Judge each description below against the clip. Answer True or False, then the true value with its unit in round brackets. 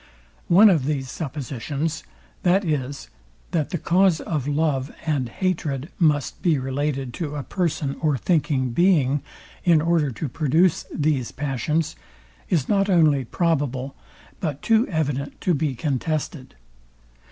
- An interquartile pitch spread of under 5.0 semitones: True (3.5 semitones)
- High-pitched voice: False (150 Hz)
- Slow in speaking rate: True (130 wpm)